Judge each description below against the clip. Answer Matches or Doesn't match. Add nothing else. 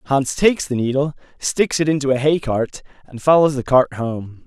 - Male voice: Matches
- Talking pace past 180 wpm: Matches